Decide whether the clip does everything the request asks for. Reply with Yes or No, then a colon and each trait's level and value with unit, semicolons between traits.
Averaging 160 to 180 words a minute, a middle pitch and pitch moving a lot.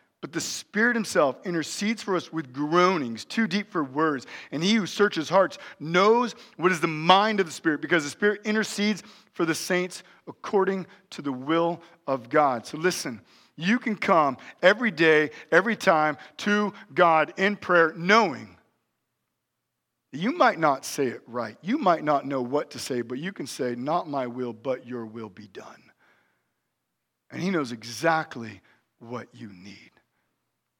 Yes: average, 170 wpm; medium, 170 Hz; wide, 6.1 semitones